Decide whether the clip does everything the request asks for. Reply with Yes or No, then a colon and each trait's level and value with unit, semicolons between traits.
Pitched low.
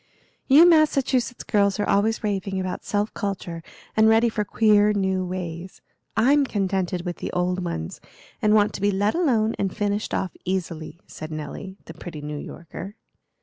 No: high, 200 Hz